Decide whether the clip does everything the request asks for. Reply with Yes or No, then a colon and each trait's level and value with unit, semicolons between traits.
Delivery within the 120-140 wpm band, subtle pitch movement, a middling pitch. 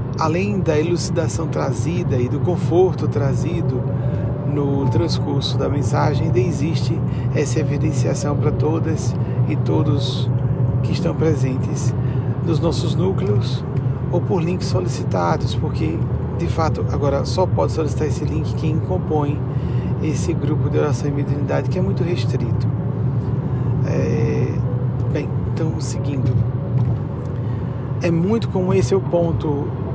No: average, 125 wpm; narrow, 2.2 semitones; low, 130 Hz